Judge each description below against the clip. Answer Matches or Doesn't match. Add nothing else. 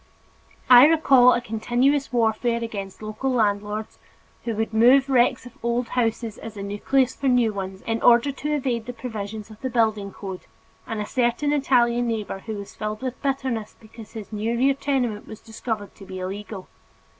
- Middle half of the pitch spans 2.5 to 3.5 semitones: Matches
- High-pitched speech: Matches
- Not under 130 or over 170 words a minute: Doesn't match